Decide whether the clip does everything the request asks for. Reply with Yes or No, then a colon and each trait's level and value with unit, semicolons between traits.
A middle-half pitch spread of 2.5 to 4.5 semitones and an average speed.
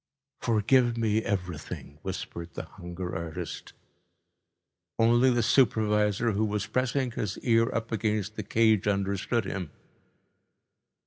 No: average, 2.9 semitones; slow, 115 wpm